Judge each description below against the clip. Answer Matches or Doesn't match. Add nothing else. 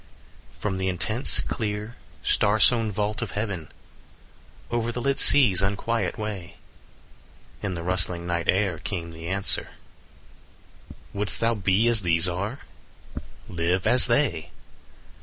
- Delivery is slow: Matches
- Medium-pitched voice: Doesn't match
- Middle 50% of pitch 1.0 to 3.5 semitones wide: Doesn't match